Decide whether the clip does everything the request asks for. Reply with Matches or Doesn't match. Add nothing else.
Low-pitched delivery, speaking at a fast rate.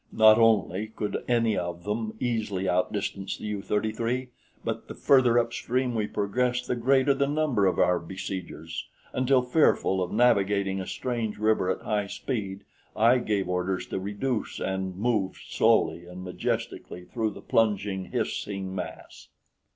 Doesn't match